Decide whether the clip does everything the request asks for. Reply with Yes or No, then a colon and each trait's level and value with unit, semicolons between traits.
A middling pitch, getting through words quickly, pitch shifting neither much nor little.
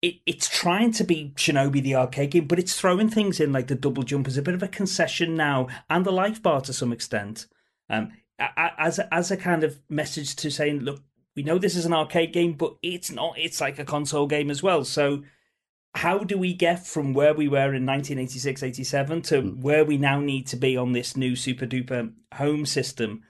Yes: medium, 145 Hz; fast, 220 wpm; average, 4.1 semitones